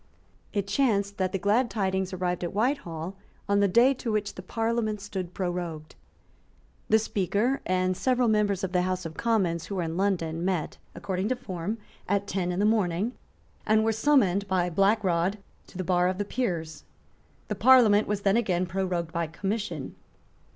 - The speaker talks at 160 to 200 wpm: Yes, average, 180 wpm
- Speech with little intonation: No, average, 3.2 semitones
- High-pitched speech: Yes, high, 195 Hz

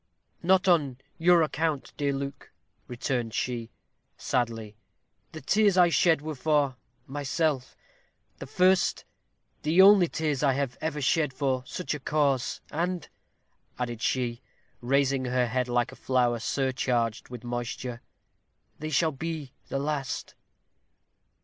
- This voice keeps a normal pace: No, slow, 130 wpm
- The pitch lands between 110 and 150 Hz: Yes, medium, 140 Hz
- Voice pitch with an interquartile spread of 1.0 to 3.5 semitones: No, average, 4.1 semitones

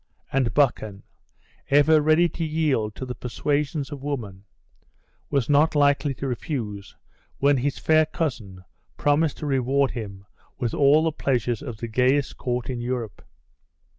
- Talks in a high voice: No, low, 135 Hz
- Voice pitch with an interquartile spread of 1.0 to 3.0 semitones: No, average, 3.6 semitones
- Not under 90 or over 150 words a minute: Yes, average, 145 wpm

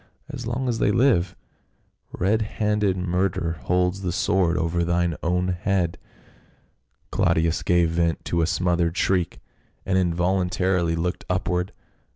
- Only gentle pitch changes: Yes, narrow, 1.9 semitones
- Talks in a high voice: No, very low, 90 Hz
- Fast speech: No, slow, 135 wpm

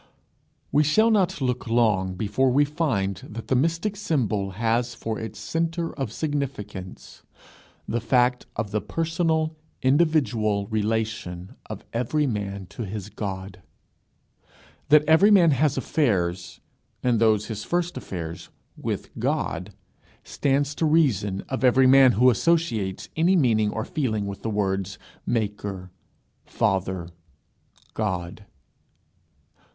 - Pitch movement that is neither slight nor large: No, wide, 6.7 semitones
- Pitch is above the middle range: No, low, 115 Hz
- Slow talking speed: Yes, slow, 125 wpm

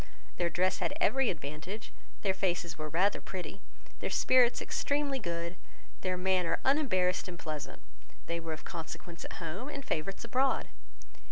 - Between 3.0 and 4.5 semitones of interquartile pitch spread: No, wide, 5.5 semitones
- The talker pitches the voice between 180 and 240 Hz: Yes, medium, 185 Hz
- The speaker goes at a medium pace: Yes, average, 150 wpm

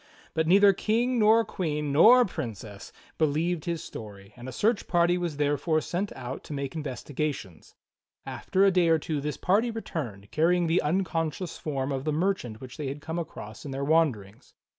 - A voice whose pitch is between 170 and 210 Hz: No, medium, 155 Hz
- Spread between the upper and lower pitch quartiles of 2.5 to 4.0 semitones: No, average, 4.8 semitones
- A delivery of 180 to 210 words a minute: Yes, average, 185 wpm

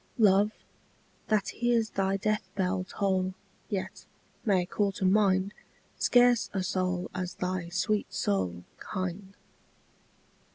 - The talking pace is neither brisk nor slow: No, slow, 115 wpm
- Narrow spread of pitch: Yes, narrow, 2.1 semitones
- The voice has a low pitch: No, high, 190 Hz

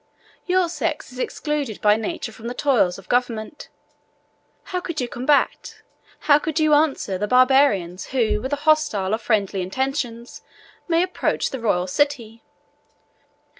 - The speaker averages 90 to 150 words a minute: Yes, average, 140 wpm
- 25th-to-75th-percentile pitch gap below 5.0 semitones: No, wide, 5.5 semitones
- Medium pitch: No, very high, 250 Hz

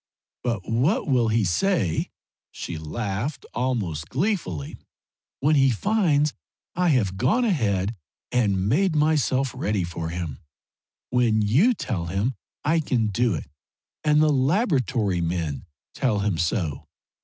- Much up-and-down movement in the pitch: Yes, wide, 7.9 semitones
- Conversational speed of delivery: No, slow, 130 wpm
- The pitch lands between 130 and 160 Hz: No, low, 120 Hz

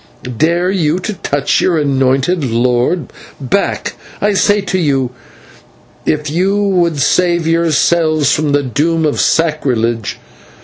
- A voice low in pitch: No, medium, 155 Hz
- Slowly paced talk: Yes, slow, 125 wpm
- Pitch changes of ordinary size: Yes, average, 4.2 semitones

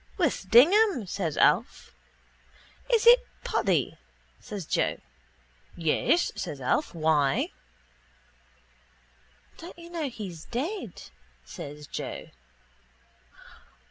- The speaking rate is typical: No, slow, 85 wpm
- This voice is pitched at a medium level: No, high, 220 Hz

